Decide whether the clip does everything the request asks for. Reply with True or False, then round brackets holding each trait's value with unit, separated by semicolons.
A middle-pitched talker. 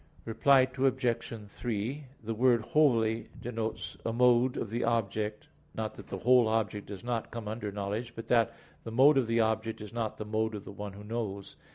False (115 Hz)